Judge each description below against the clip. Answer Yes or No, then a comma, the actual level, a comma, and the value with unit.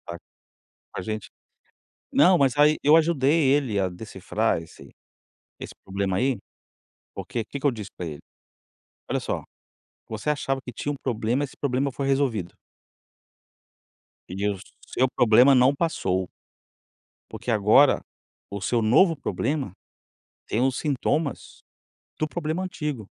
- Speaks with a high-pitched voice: No, low, 130 Hz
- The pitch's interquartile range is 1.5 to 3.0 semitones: No, average, 5.3 semitones